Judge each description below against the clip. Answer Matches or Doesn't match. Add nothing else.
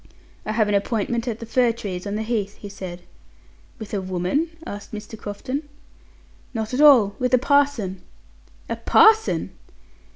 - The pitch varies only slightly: Doesn't match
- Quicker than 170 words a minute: Doesn't match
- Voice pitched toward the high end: Matches